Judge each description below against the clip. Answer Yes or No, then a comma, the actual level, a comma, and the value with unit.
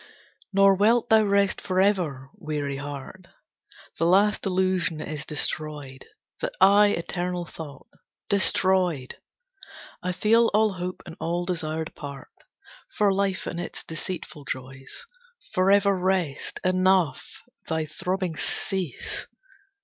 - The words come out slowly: Yes, slow, 110 wpm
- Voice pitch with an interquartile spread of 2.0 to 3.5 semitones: No, average, 4.1 semitones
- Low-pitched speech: No, medium, 180 Hz